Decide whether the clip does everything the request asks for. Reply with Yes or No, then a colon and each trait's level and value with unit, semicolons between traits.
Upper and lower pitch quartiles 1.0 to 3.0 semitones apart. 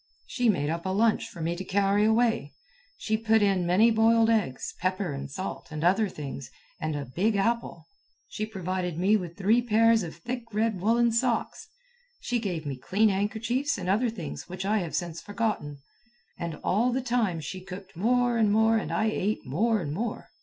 No: average, 4.4 semitones